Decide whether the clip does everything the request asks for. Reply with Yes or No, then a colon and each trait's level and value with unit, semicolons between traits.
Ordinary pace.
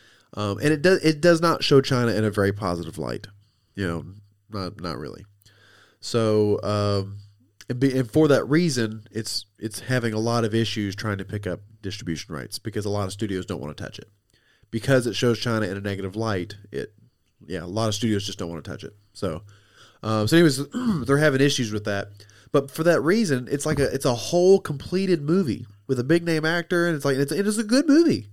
No: fast, 220 wpm